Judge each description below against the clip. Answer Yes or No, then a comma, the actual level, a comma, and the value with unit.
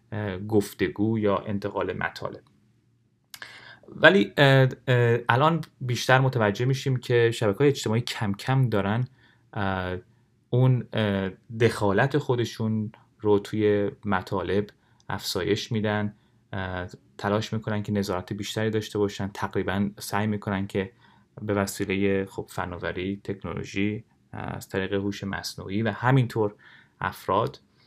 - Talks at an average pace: No, slow, 100 wpm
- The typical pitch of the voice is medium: No, low, 105 Hz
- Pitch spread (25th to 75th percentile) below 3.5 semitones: Yes, average, 3.0 semitones